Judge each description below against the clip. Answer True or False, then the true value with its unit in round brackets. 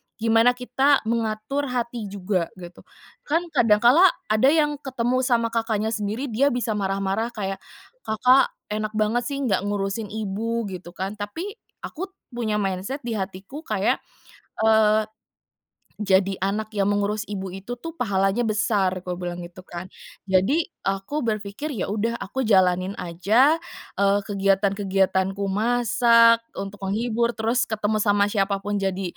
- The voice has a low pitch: False (215 Hz)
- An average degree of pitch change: True (3.3 semitones)